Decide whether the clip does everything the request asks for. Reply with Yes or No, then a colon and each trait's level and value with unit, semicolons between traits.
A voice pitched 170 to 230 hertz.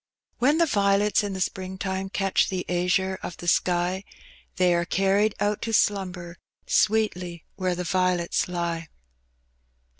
Yes: medium, 185 Hz